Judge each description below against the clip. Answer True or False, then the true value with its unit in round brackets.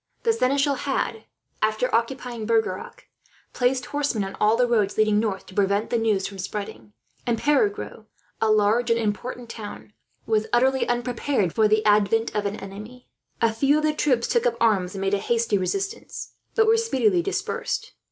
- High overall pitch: True (230 Hz)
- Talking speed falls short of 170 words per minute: False (175 wpm)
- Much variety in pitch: False (4.2 semitones)